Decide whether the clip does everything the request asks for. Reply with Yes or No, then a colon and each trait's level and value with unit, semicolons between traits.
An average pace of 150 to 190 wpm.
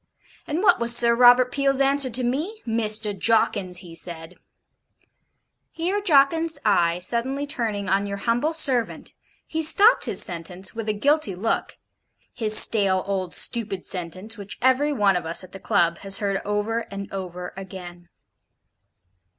Yes: average, 155 wpm